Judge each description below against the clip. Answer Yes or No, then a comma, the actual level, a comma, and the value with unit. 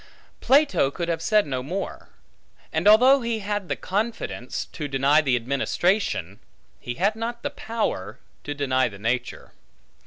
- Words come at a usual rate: Yes, average, 150 wpm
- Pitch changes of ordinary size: No, wide, 8.7 semitones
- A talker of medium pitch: Yes, medium, 170 Hz